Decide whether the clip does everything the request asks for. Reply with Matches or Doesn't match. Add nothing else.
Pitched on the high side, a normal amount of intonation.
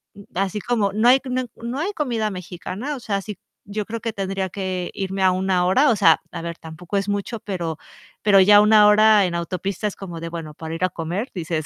Matches